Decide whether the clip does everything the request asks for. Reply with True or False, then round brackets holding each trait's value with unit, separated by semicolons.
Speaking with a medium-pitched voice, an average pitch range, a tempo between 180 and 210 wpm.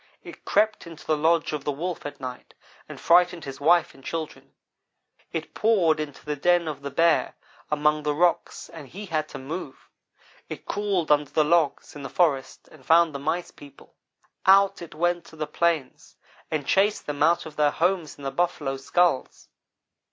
True (155 Hz; 3.0 semitones; 185 wpm)